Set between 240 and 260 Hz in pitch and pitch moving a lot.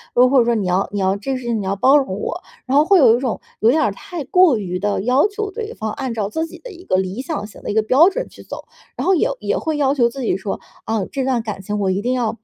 Yes: high, 245 Hz; wide, 6.2 semitones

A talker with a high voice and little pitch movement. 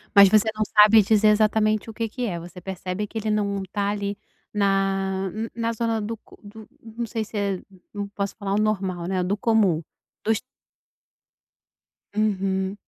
Yes: high, 205 Hz; narrow, 2.0 semitones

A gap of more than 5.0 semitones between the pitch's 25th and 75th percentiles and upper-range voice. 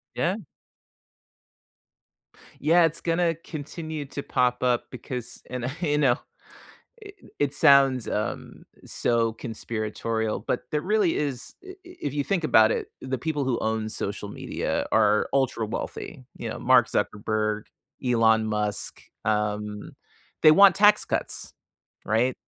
No: wide, 5.6 semitones; low, 125 Hz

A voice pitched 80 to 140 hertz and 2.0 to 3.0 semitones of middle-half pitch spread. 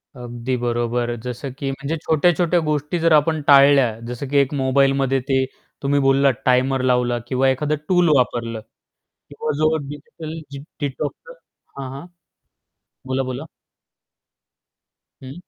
Yes: low, 135 Hz; average, 2.7 semitones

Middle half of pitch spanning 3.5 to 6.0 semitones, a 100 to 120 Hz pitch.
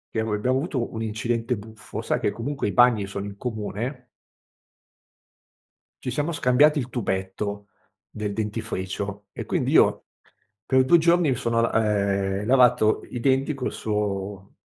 Yes: average, 3.8 semitones; low, 110 Hz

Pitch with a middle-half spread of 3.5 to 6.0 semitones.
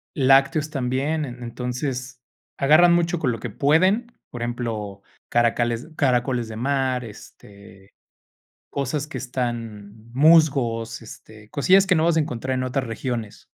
Yes: average, 3.8 semitones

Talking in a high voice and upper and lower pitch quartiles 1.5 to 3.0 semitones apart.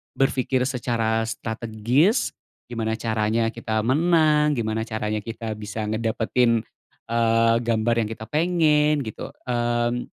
No: low, 115 Hz; narrow, 2.6 semitones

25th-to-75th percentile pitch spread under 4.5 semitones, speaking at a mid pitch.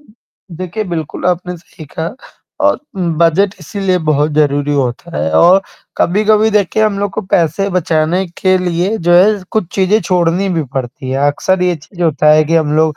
Yes: average, 3.9 semitones; medium, 175 Hz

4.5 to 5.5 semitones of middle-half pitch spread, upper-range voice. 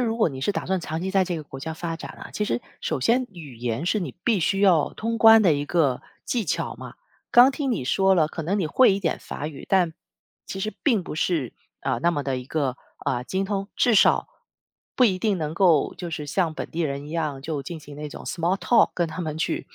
No: average, 4.8 semitones; medium, 170 Hz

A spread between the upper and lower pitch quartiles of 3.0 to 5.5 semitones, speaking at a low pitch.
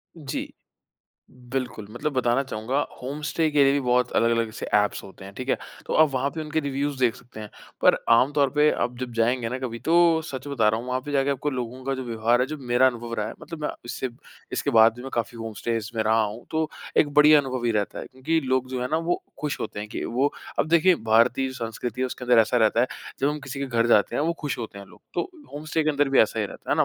Yes: average, 3.6 semitones; low, 130 Hz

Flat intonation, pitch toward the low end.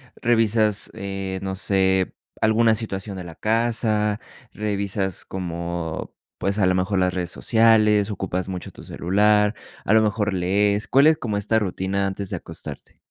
Yes: narrow, 2.3 semitones; low, 100 Hz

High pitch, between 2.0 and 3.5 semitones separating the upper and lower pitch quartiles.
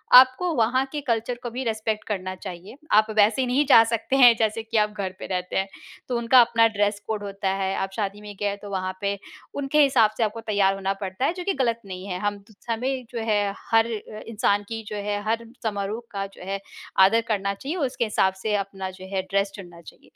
Yes: high, 210 Hz; average, 2.9 semitones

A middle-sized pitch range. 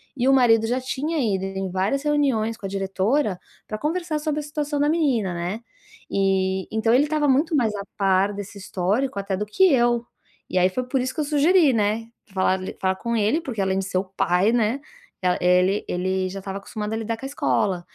No: wide, 6.0 semitones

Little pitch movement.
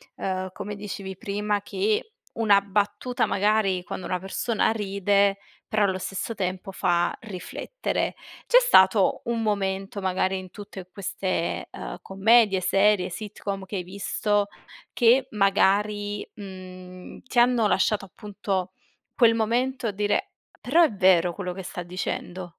Yes: narrow, 2.1 semitones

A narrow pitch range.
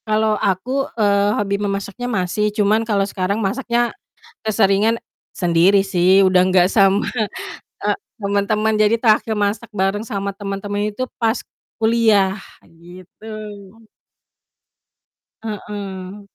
Yes: narrow, 2.1 semitones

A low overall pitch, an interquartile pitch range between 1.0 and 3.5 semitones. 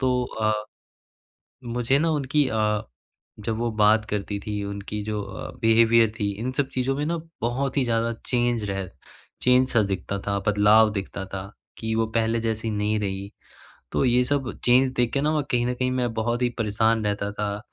Yes: low, 115 Hz; average, 3.1 semitones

